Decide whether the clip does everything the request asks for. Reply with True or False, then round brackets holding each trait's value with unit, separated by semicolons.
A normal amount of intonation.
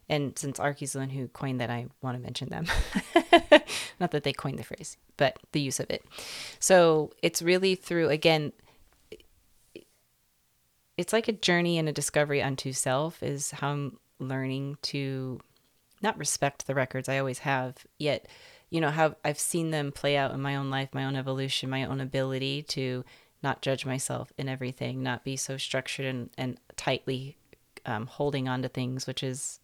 False (2.3 semitones)